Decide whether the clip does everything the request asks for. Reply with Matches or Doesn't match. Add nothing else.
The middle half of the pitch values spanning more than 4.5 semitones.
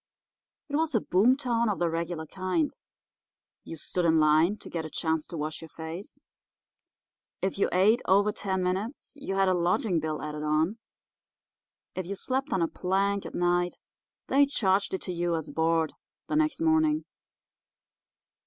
Matches